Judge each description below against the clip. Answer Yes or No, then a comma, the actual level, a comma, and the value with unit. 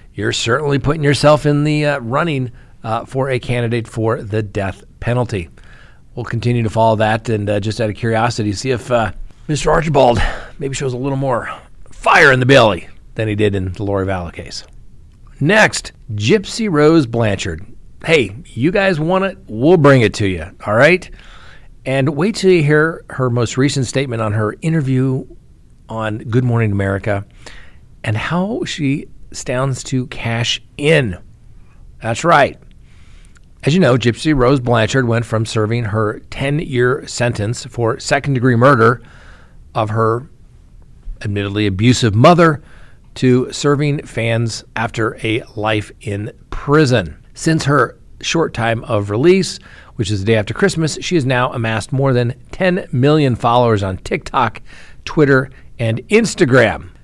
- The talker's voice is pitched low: Yes, low, 120 Hz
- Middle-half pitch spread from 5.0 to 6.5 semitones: No, average, 4.4 semitones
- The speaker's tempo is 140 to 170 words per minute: Yes, average, 150 wpm